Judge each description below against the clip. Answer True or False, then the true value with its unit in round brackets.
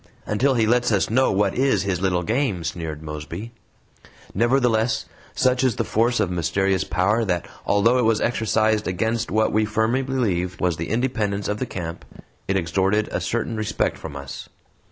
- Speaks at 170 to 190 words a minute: True (175 wpm)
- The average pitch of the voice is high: False (105 Hz)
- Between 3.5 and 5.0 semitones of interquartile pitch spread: True (4.5 semitones)